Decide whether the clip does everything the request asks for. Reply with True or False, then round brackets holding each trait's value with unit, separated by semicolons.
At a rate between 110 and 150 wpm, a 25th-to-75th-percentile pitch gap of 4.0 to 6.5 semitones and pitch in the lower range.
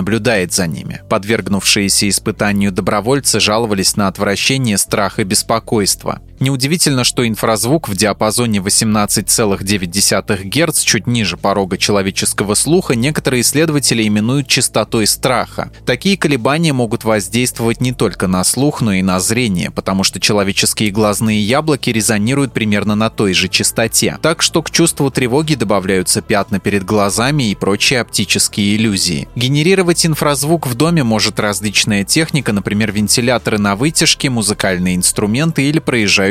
True (130 wpm; 4.9 semitones; 110 Hz)